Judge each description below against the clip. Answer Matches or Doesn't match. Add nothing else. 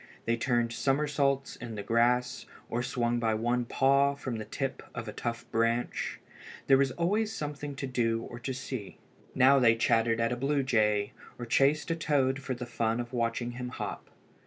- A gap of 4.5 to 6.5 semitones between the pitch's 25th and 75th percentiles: Doesn't match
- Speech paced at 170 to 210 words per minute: Matches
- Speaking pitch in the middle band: Doesn't match